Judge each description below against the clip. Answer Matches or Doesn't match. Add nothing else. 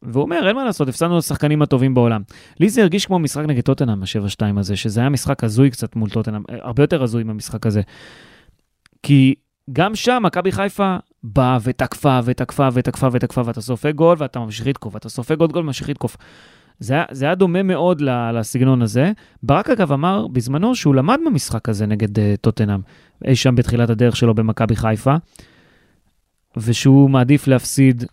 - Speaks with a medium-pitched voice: Doesn't match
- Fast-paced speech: Matches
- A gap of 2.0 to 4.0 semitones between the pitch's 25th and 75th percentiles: Doesn't match